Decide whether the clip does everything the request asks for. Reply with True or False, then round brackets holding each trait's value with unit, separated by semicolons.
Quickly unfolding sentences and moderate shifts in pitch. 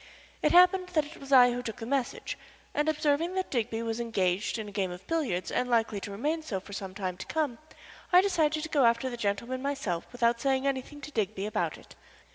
False (225 wpm; 5.9 semitones)